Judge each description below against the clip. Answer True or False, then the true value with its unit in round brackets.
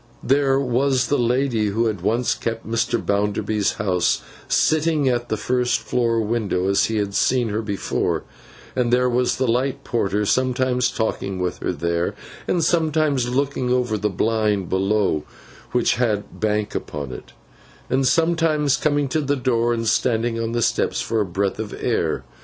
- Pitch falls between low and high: False (120 Hz)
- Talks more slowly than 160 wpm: False (165 wpm)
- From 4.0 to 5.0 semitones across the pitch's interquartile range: False (3.6 semitones)